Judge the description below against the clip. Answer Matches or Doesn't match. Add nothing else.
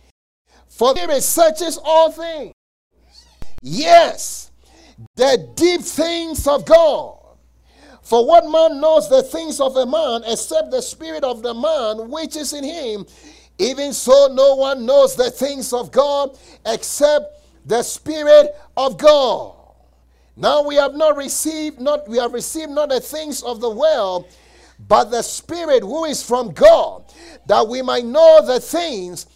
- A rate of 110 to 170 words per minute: Matches